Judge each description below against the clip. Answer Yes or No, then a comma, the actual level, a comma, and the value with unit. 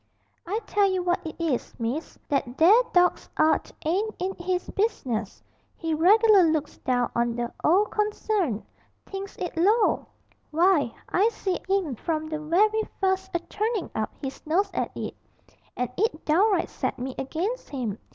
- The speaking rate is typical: Yes, average, 160 wpm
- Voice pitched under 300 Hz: No, very high, 350 Hz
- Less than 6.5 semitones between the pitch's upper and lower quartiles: Yes, wide, 5.4 semitones